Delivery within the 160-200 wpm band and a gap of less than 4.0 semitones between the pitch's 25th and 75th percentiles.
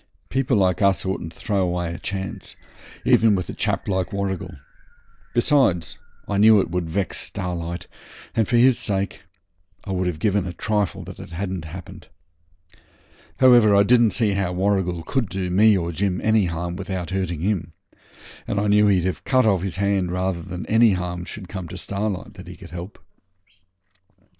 Yes: average, 175 wpm; narrow, 2.6 semitones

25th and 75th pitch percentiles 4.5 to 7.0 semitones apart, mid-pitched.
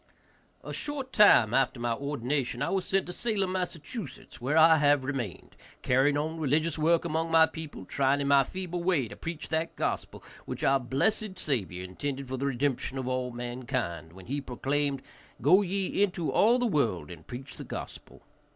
Yes: average, 4.9 semitones; medium, 145 Hz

